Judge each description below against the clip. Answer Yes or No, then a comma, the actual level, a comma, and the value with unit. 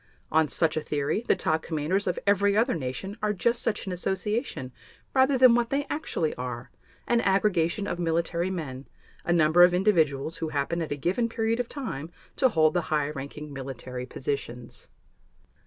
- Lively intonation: Yes, wide, 5.9 semitones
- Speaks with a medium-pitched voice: Yes, medium, 170 Hz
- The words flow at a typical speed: Yes, average, 175 wpm